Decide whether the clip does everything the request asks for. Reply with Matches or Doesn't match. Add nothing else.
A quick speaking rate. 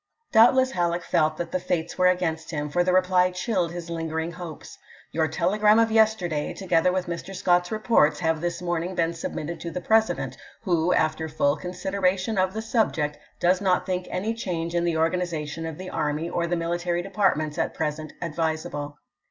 Doesn't match